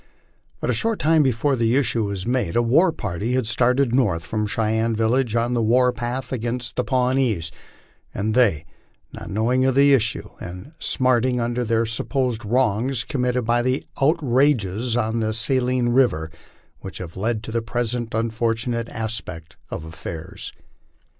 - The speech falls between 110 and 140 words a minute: No, average, 160 wpm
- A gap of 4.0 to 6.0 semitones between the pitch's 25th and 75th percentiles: No, average, 2.7 semitones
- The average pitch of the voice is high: No, low, 120 Hz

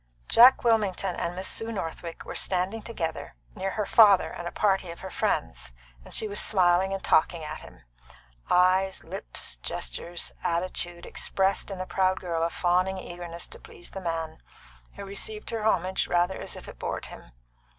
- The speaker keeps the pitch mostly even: Yes, narrow, 2.2 semitones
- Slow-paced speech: No, average, 175 wpm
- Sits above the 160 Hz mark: Yes, medium, 185 Hz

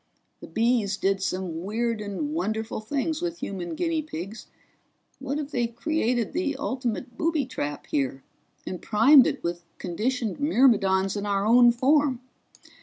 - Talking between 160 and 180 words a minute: No, average, 145 wpm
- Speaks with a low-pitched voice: No, high, 235 Hz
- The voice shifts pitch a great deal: Yes, wide, 6.2 semitones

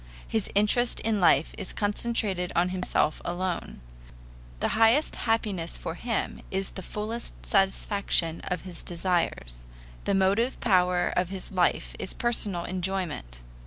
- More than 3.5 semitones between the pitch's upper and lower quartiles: No, average, 3.2 semitones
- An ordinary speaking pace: No, slow, 130 wpm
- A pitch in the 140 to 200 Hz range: Yes, high, 190 Hz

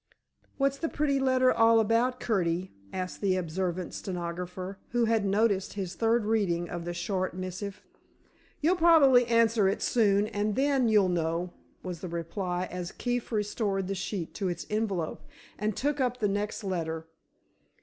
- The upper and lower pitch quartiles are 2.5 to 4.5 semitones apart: Yes, average, 4.2 semitones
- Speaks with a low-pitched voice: No, high, 200 Hz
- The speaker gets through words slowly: No, average, 160 wpm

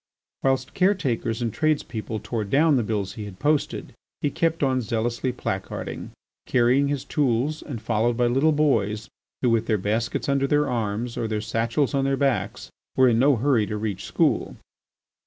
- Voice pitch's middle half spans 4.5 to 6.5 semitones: No, average, 3.9 semitones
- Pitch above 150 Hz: No, low, 120 Hz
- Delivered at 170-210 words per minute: Yes, average, 175 wpm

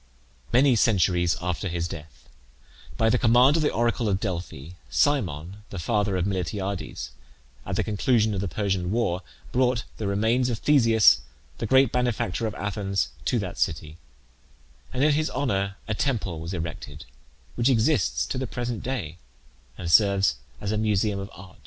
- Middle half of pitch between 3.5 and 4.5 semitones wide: No, average, 5.2 semitones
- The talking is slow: No, average, 145 wpm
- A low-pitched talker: Yes, low, 105 Hz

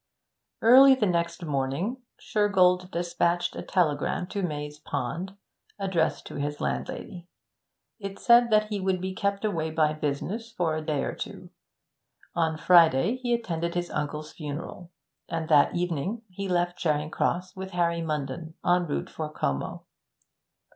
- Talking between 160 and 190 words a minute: No, average, 145 wpm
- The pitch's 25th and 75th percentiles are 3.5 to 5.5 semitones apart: Yes, average, 3.8 semitones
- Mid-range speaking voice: Yes, medium, 175 Hz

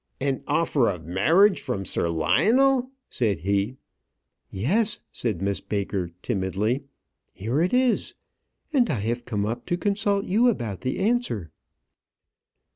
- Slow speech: Yes, slow, 130 wpm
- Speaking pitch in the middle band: No, low, 120 Hz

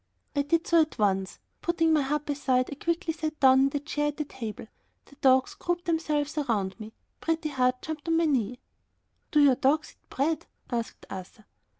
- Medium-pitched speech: No, very high, 290 Hz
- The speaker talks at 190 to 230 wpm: Yes, average, 195 wpm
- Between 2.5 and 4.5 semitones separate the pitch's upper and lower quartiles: Yes, average, 3.9 semitones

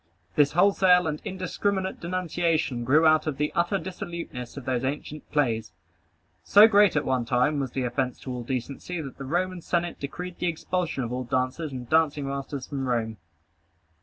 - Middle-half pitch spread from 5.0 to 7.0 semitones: Yes, average, 5.3 semitones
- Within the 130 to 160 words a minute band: No, average, 175 wpm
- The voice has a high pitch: No, medium, 150 Hz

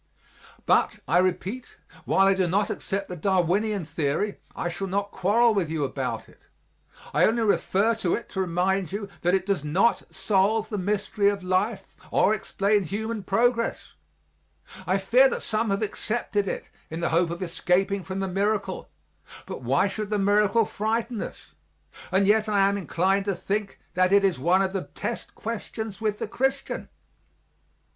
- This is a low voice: No, high, 195 Hz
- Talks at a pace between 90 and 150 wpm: No, average, 170 wpm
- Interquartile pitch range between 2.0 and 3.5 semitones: Yes, narrow, 2.5 semitones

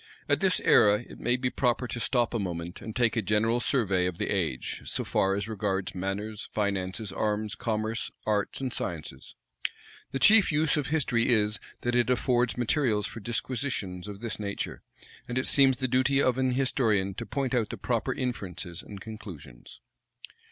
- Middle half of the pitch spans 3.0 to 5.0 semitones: Yes, average, 4.0 semitones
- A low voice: Yes, low, 110 Hz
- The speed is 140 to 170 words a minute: No, average, 180 wpm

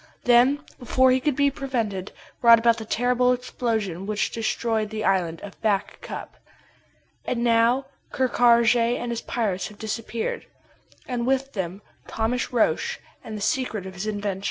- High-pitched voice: Yes, high, 230 Hz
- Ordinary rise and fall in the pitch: Yes, average, 3.0 semitones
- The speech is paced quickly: No, average, 155 wpm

